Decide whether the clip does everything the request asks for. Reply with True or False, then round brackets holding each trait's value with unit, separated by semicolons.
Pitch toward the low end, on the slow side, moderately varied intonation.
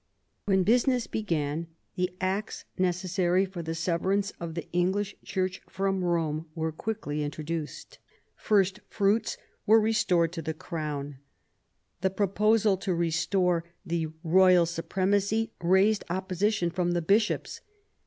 False (185 Hz; 125 wpm; 3.2 semitones)